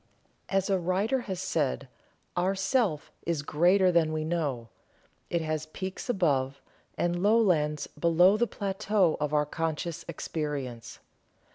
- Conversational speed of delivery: No, slow, 130 wpm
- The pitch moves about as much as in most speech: Yes, average, 4.0 semitones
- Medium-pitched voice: Yes, medium, 170 Hz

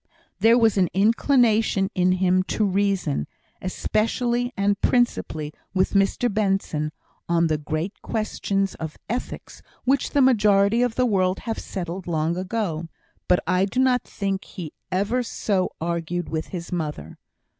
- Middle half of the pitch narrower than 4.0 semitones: No, average, 4.4 semitones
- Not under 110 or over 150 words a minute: Yes, average, 145 wpm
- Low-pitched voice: No, high, 195 Hz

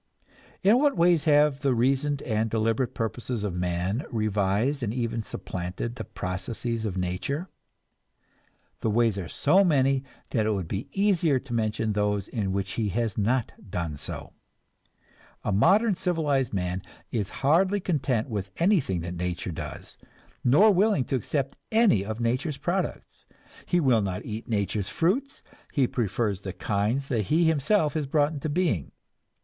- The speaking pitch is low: Yes, low, 120 Hz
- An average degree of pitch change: No, wide, 6.7 semitones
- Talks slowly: No, average, 155 wpm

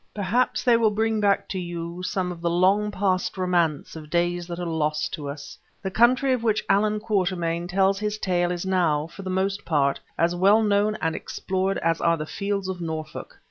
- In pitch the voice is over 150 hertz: Yes, medium, 185 Hz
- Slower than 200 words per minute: No, fast, 205 wpm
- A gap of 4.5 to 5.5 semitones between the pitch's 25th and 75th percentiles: No, average, 3.2 semitones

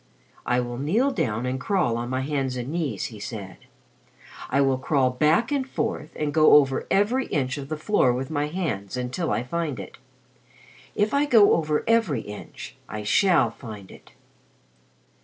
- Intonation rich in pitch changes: Yes, wide, 5.7 semitones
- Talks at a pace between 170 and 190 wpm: Yes, average, 175 wpm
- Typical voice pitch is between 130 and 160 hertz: Yes, medium, 140 Hz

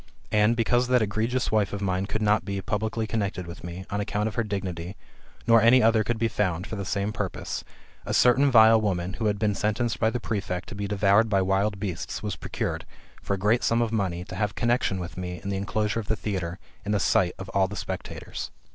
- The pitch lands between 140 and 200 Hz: No, low, 105 Hz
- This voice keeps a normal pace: No, fast, 235 wpm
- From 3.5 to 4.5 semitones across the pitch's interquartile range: No, narrow, 2.5 semitones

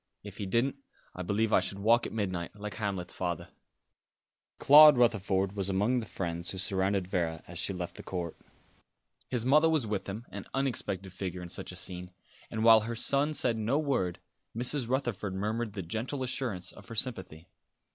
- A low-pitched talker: Yes, low, 105 Hz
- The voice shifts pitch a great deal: No, average, 4.3 semitones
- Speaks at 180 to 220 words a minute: Yes, average, 185 wpm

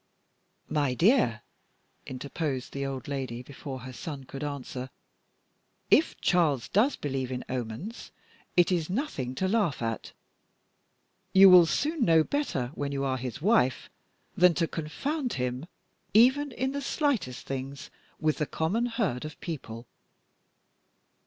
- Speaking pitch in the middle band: Yes, medium, 150 Hz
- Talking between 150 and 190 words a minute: No, slow, 135 wpm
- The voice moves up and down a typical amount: No, wide, 7.1 semitones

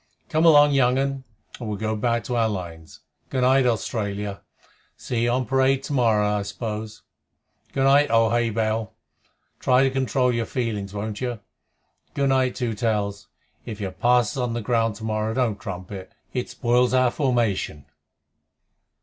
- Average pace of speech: Yes, average, 165 wpm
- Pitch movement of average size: Yes, average, 3.4 semitones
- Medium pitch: No, low, 115 Hz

